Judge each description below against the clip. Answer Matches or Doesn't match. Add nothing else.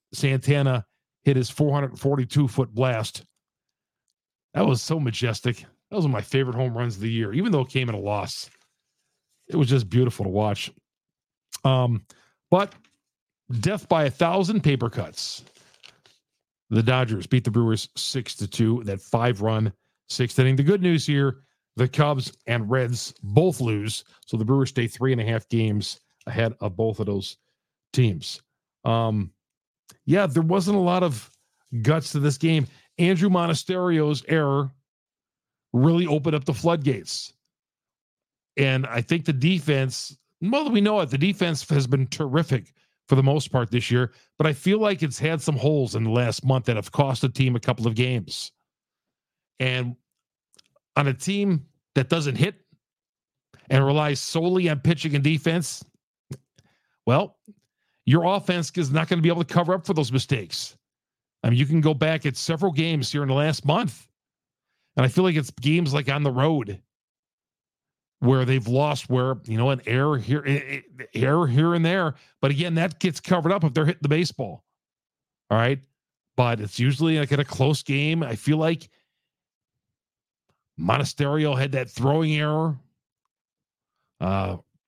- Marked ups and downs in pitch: Doesn't match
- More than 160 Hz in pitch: Doesn't match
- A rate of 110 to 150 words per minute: Doesn't match